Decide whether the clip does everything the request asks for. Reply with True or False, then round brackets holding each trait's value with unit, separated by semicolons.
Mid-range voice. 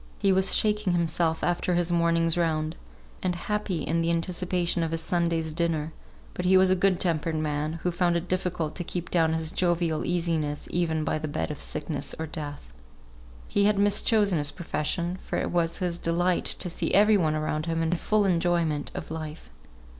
True (170 Hz)